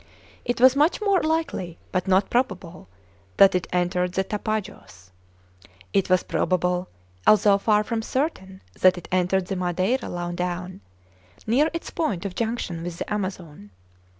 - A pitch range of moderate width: Yes, average, 3.8 semitones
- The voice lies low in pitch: No, high, 190 Hz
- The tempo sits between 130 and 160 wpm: Yes, average, 150 wpm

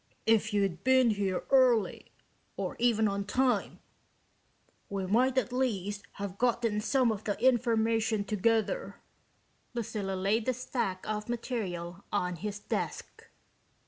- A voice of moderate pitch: No, high, 220 Hz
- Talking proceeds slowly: Yes, slow, 125 wpm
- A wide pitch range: No, average, 3.3 semitones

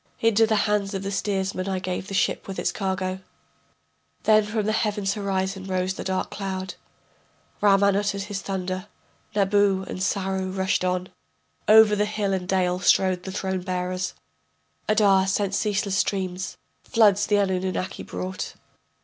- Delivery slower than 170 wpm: Yes, average, 150 wpm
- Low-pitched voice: No, high, 195 Hz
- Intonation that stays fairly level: Yes, narrow, 1.5 semitones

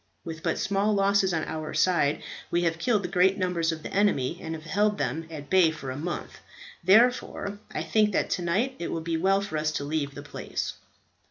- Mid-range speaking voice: Yes, medium, 175 Hz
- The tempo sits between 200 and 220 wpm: Yes, fast, 205 wpm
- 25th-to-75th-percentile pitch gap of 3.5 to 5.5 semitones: Yes, average, 3.8 semitones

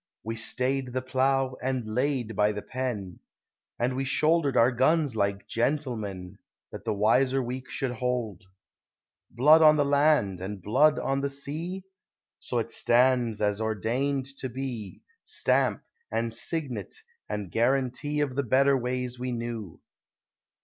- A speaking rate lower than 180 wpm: Yes, average, 140 wpm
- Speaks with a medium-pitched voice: No, low, 125 Hz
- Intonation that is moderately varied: Yes, average, 3.5 semitones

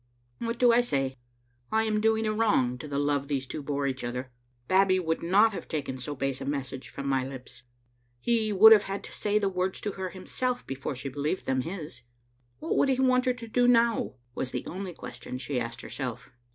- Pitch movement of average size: No, wide, 8.5 semitones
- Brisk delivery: Yes, fast, 220 wpm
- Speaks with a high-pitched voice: No, medium, 165 Hz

